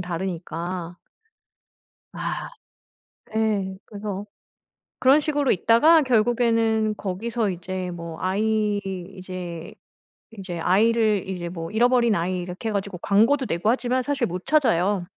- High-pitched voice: Yes, high, 205 Hz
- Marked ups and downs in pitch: No, average, 4.2 semitones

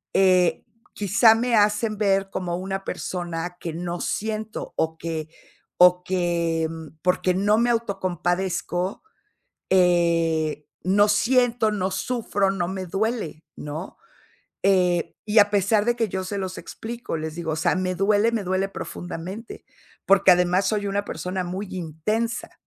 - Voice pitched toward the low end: No, high, 190 Hz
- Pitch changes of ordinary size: Yes, average, 3.0 semitones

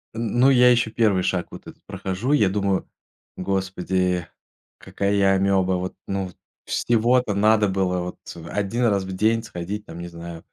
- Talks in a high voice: No, low, 100 Hz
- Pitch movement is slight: No, average, 3.1 semitones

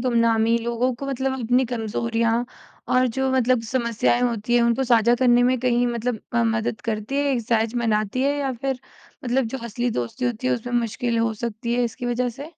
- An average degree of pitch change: No, narrow, 1.8 semitones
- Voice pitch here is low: No, high, 240 Hz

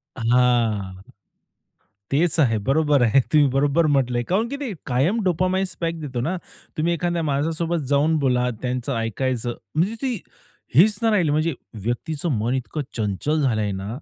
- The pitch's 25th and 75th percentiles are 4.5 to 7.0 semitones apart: Yes, wide, 5.4 semitones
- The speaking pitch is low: No, medium, 145 Hz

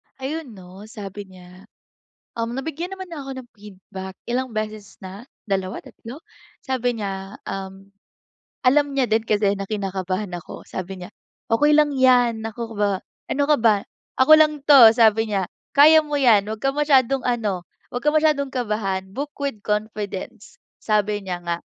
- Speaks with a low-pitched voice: No, high, 220 Hz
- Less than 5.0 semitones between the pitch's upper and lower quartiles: No, average, 5.3 semitones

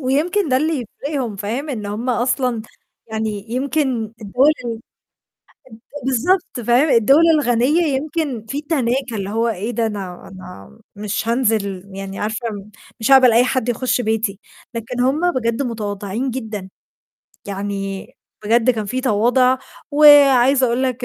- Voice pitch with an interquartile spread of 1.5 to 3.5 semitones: No, average, 3.9 semitones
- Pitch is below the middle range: No, high, 240 Hz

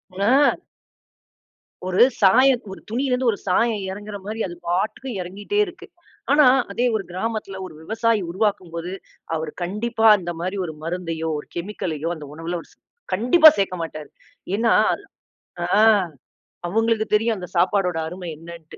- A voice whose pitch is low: No, high, 195 Hz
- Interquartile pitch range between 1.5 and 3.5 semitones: No, average, 4.6 semitones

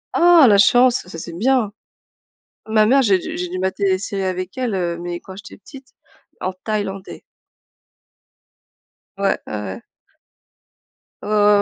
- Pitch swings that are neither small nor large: Yes, average, 3.1 semitones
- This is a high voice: Yes, high, 200 Hz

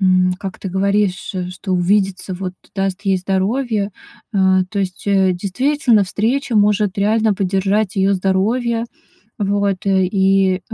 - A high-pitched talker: Yes, high, 195 Hz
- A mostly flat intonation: Yes, narrow, 1.8 semitones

